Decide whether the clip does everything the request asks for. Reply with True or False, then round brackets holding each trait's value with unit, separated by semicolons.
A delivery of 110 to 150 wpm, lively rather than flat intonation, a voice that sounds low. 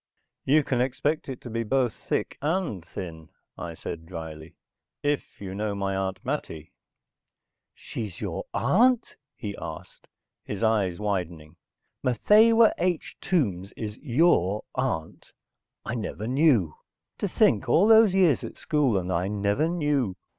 True (140 wpm; 8.0 semitones; 110 Hz)